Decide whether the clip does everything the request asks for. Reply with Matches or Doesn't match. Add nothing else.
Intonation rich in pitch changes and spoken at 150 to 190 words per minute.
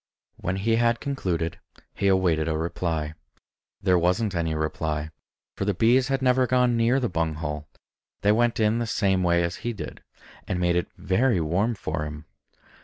Matches